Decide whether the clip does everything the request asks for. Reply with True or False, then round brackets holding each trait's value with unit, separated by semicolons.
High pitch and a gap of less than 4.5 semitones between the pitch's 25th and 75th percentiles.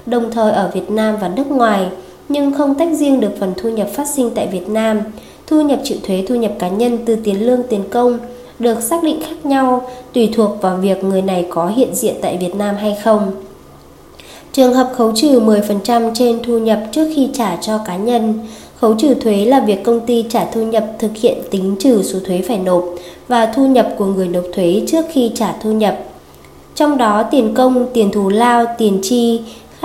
True (225 Hz; 3.5 semitones)